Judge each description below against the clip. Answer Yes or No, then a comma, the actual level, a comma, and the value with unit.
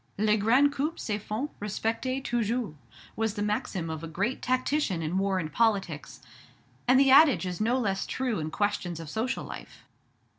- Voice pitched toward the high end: Yes, high, 215 Hz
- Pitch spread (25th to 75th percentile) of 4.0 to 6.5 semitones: Yes, average, 5.1 semitones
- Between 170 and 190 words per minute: Yes, average, 175 wpm